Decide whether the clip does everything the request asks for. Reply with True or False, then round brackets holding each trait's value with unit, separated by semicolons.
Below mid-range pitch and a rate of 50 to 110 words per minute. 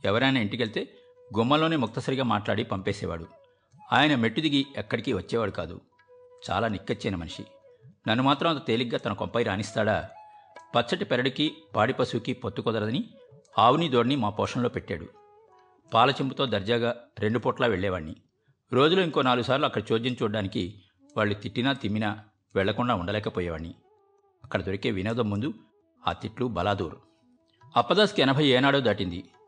False (120 Hz; 120 wpm)